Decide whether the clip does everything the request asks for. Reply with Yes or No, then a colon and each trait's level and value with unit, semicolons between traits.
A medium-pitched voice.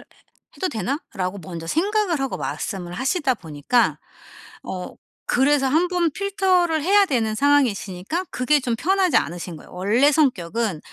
No: very high, 265 Hz